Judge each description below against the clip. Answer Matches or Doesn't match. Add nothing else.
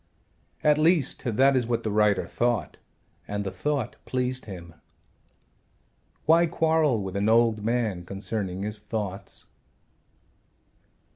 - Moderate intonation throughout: Matches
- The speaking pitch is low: Matches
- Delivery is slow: Matches